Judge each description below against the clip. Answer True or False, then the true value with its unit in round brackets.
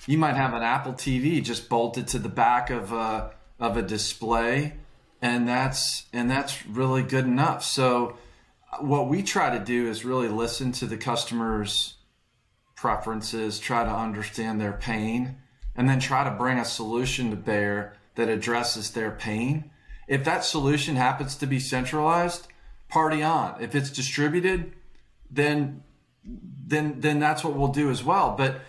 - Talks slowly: False (160 wpm)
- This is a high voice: False (130 Hz)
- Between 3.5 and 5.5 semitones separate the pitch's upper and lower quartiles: True (3.9 semitones)